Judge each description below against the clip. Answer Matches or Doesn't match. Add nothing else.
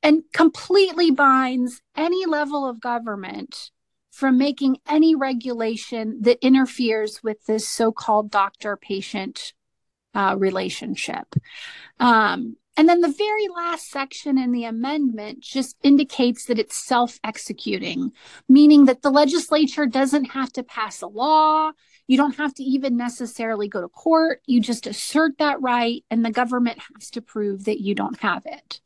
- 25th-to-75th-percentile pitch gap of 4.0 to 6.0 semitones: Matches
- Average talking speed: Matches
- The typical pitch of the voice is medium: Doesn't match